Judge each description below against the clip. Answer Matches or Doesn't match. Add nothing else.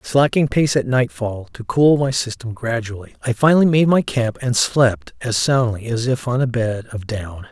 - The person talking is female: Doesn't match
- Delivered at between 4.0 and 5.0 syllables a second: Matches